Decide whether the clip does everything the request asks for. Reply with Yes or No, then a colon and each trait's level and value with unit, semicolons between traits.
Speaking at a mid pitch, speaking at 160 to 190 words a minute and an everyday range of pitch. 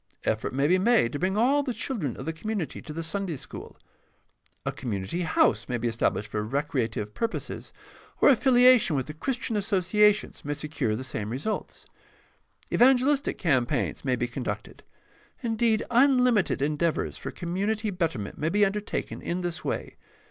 No: medium, 175 Hz; average, 165 wpm; wide, 8.6 semitones